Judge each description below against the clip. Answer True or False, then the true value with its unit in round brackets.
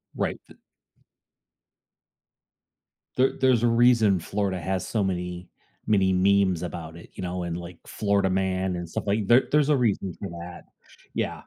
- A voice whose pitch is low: True (95 Hz)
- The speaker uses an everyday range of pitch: True (3.3 semitones)